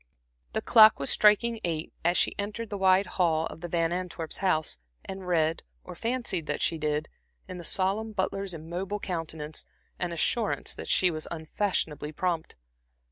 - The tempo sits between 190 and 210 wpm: No, average, 165 wpm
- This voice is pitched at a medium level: Yes, medium, 175 Hz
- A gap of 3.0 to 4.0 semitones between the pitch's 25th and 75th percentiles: Yes, average, 3.6 semitones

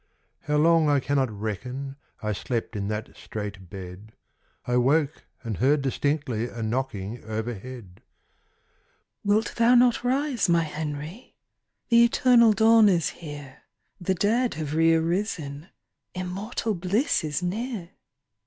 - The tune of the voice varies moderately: No, wide, 8.8 semitones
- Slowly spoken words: Yes, slow, 125 wpm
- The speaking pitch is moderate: Yes, medium, 150 Hz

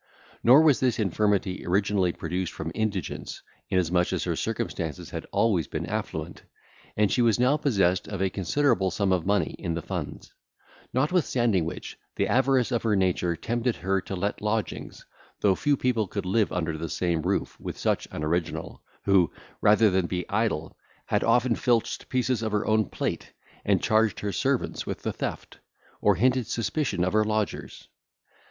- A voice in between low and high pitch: No, low, 100 Hz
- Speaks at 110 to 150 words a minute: No, average, 170 wpm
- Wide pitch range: No, average, 4.4 semitones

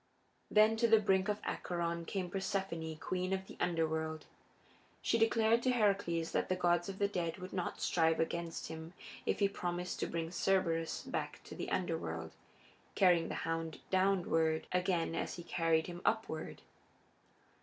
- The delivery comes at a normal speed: Yes, average, 160 wpm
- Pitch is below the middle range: No, medium, 175 Hz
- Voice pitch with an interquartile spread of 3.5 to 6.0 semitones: No, average, 2.9 semitones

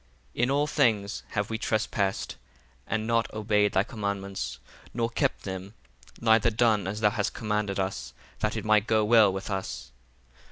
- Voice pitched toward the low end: Yes, low, 105 Hz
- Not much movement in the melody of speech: Yes, narrow, 2.1 semitones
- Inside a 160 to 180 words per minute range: Yes, average, 165 wpm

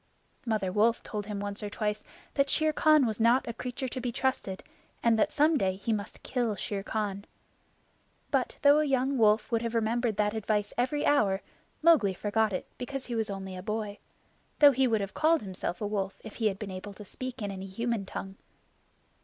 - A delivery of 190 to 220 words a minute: Yes, fast, 205 wpm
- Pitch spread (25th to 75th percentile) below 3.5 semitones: No, average, 3.8 semitones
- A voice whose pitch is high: Yes, high, 220 Hz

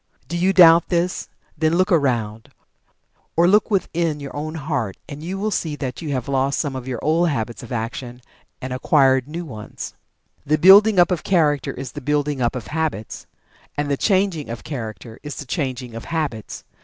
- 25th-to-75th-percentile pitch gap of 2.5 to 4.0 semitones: No, average, 4.9 semitones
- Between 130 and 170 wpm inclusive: No, average, 195 wpm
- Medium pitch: Yes, medium, 145 Hz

